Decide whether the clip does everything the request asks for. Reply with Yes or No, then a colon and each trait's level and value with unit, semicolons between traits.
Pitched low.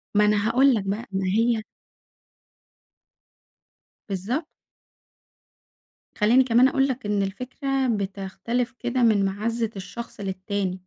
No: high, 215 Hz